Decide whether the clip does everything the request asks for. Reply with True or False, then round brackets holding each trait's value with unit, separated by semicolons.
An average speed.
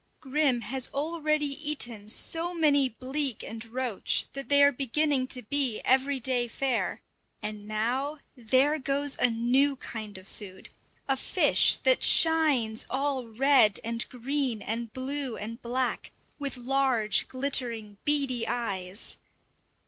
False (130 wpm)